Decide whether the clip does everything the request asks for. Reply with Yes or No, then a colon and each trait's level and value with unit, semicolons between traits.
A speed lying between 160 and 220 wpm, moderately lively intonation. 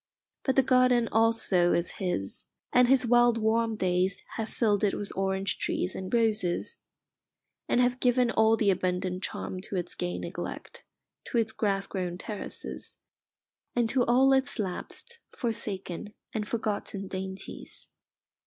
No: average, 145 wpm; average, 4.2 semitones